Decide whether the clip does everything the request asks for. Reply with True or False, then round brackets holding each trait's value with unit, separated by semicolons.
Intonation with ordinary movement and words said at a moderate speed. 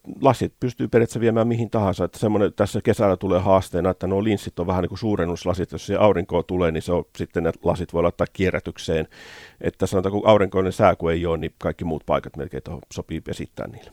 False (3.1 semitones; 200 wpm)